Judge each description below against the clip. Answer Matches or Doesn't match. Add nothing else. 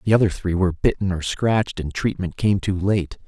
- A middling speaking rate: Doesn't match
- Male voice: Matches